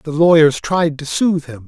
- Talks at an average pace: No, fast, 215 wpm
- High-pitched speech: No, medium, 155 Hz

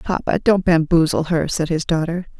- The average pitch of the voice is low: No, medium, 170 Hz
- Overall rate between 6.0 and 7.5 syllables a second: No, 5.0 syllables/s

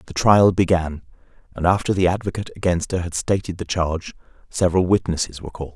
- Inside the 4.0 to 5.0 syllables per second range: No, 6.5 syllables/s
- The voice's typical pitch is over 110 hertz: No, very low, 90 Hz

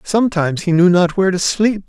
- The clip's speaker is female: No, male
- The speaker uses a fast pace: Yes, fast, 225 wpm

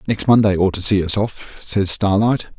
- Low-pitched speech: Yes, low, 100 Hz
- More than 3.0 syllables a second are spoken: Yes, 4.8 syllables/s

